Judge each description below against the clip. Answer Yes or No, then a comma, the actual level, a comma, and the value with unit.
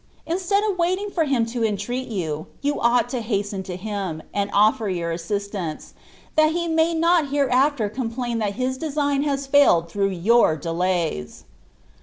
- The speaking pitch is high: Yes, high, 235 Hz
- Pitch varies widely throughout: Yes, wide, 6.6 semitones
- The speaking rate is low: No, average, 160 wpm